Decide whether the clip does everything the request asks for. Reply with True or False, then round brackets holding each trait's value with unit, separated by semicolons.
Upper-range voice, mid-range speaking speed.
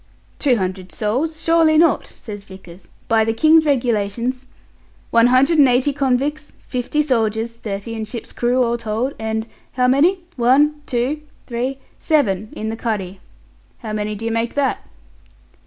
True (240 Hz; 155 wpm)